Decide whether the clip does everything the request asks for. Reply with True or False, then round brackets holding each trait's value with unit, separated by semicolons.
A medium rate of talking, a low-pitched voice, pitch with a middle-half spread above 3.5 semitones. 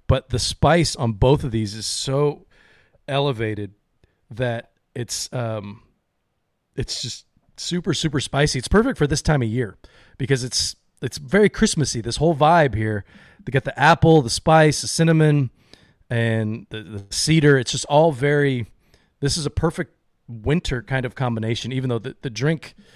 True (160 wpm; 130 Hz; 4.7 semitones)